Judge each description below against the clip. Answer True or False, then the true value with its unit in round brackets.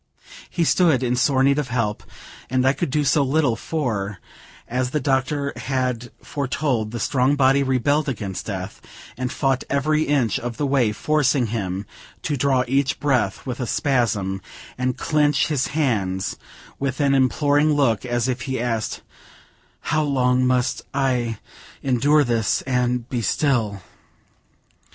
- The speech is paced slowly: False (150 wpm)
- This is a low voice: True (130 Hz)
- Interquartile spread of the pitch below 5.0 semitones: True (2.9 semitones)